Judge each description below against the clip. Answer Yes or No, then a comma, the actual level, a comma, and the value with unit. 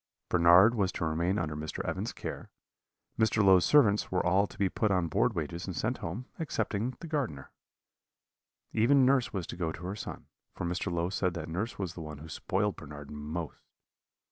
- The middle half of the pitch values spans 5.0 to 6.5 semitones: No, average, 4.6 semitones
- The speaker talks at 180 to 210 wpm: Yes, average, 195 wpm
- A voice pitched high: No, very low, 90 Hz